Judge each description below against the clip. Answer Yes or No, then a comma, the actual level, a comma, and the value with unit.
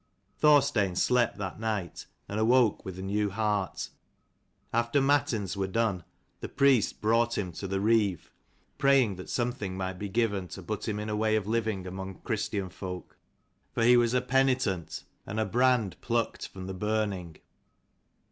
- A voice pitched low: Yes, low, 105 Hz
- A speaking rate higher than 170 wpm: No, average, 165 wpm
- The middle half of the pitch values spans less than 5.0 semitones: Yes, average, 3.6 semitones